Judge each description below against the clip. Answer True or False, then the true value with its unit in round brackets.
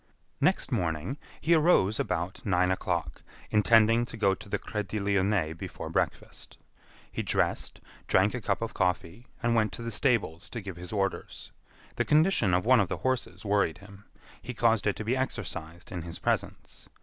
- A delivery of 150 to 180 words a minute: True (175 wpm)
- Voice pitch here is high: False (100 Hz)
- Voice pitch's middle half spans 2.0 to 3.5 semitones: False (4.2 semitones)